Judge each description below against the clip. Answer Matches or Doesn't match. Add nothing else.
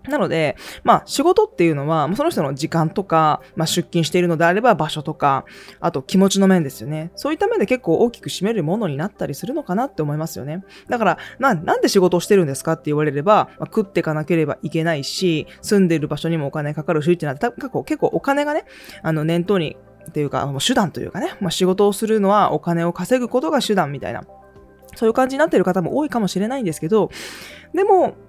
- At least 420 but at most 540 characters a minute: Matches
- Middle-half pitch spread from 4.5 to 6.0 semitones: Matches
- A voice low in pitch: Doesn't match